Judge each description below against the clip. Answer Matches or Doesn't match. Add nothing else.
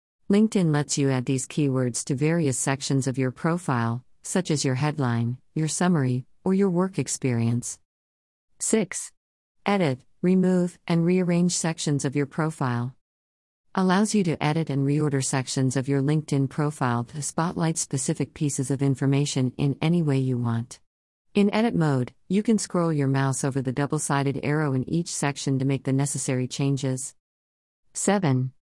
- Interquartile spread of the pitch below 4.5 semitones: Matches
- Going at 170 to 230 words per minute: Doesn't match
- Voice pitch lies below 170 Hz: Matches